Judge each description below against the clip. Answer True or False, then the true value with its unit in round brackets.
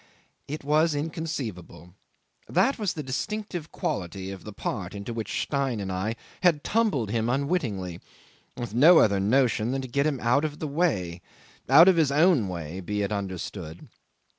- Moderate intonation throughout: False (7.8 semitones)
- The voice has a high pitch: False (125 Hz)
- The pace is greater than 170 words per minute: False (165 wpm)